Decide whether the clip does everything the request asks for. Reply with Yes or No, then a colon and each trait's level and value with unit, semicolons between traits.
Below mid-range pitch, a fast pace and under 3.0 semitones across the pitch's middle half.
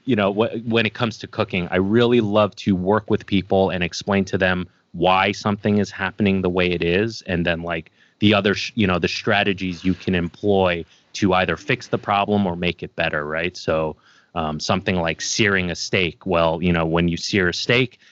No: very low, 95 Hz; fast, 215 wpm; average, 3.3 semitones